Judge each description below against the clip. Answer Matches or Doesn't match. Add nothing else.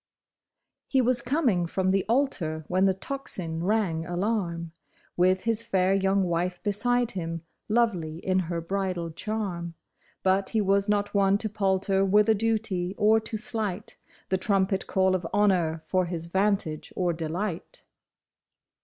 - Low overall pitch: Doesn't match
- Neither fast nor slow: Matches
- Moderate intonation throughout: Matches